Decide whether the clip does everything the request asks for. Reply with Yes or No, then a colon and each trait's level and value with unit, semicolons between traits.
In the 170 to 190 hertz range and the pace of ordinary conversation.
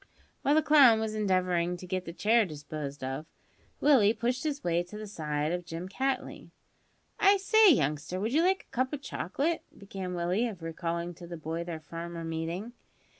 Yes: medium, 185 Hz; average, 195 wpm